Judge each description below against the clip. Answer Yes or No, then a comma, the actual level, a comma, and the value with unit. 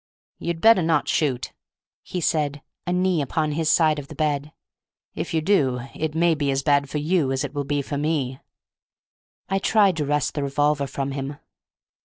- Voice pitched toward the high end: No, medium, 150 Hz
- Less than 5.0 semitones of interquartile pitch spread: Yes, narrow, 2.6 semitones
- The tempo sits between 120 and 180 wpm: No, average, 190 wpm